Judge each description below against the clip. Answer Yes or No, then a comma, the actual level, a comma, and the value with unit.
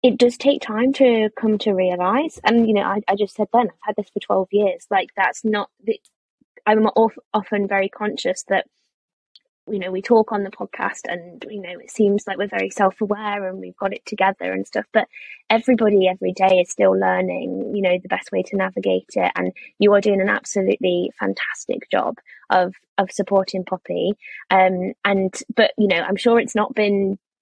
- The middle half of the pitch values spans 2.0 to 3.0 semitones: Yes, narrow, 2.6 semitones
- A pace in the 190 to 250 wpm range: Yes, average, 200 wpm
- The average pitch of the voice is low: No, high, 200 Hz